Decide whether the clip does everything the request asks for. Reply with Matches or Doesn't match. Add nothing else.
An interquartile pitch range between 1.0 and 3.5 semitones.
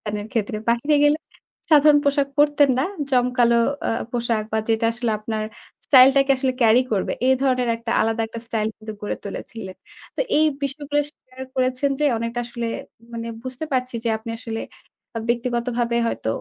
Matches